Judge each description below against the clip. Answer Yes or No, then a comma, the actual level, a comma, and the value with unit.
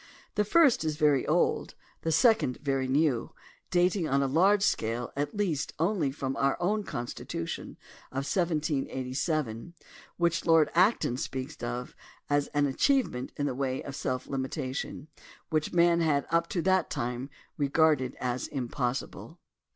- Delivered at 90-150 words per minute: Yes, average, 145 wpm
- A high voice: No, medium, 145 Hz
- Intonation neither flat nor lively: Yes, average, 4.5 semitones